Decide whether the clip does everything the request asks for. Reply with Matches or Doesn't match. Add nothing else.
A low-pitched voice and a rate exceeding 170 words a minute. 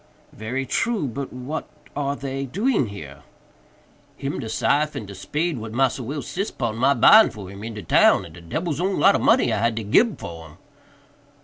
Matches